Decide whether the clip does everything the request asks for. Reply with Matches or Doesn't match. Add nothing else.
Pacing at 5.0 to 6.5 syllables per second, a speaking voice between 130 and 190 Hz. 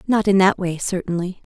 Matches